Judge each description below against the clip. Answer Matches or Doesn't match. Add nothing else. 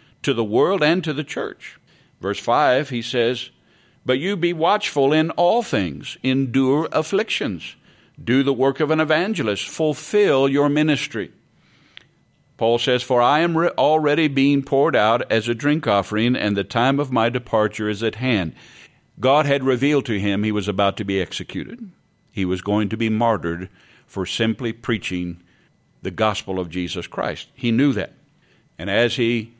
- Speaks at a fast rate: Doesn't match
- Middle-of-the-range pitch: Doesn't match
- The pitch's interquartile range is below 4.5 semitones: Doesn't match